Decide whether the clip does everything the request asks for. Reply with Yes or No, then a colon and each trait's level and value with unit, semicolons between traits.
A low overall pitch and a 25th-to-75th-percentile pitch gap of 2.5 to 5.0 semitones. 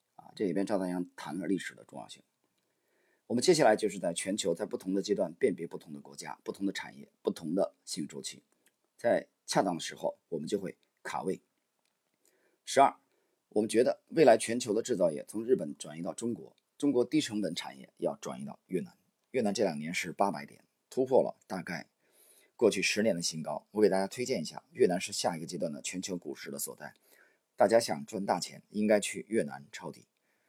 Yes: low, 105 Hz; average, 4.2 semitones